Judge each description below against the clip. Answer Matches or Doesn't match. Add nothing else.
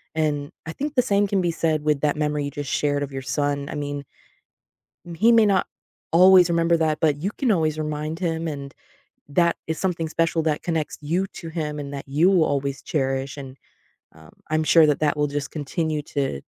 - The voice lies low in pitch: Doesn't match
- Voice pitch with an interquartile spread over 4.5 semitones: Doesn't match